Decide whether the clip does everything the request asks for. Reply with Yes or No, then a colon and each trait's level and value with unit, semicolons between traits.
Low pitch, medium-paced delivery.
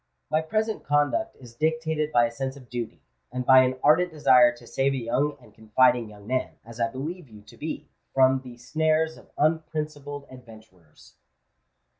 Yes: low, 130 Hz; average, 175 wpm